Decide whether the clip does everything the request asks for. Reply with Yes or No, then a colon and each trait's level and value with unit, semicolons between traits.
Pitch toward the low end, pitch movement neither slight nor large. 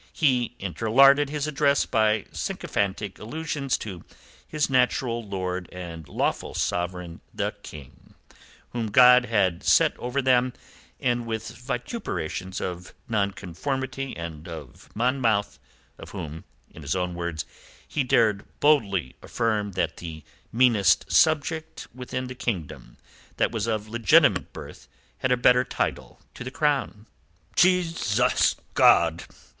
No: low, 115 Hz; wide, 6.0 semitones